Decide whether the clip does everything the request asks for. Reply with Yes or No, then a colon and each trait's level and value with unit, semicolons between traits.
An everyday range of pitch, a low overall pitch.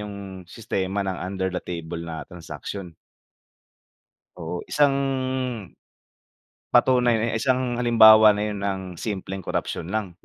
Yes: average, 3.9 semitones; low, 100 Hz